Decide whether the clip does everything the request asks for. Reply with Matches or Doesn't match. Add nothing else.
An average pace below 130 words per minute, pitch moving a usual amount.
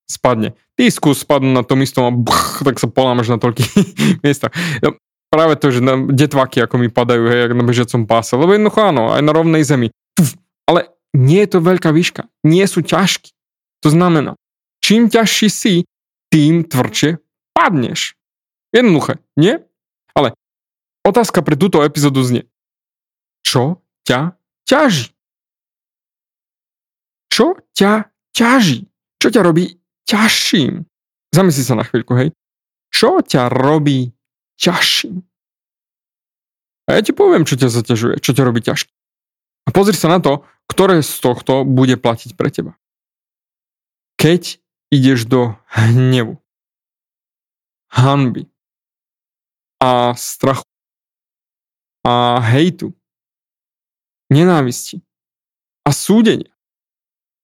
Doesn't match